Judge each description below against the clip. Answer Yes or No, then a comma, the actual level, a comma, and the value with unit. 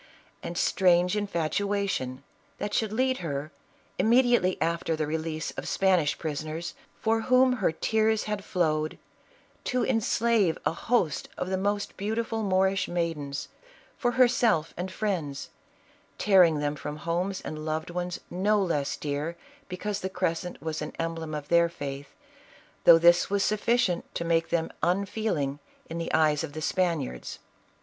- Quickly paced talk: No, average, 150 wpm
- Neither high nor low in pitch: Yes, medium, 175 Hz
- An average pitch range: Yes, average, 4.5 semitones